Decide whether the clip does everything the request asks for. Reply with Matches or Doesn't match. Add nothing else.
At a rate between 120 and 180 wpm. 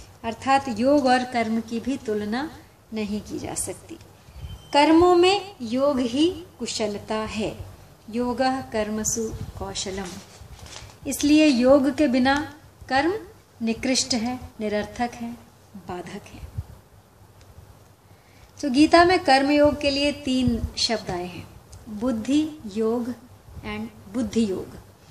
Doesn't match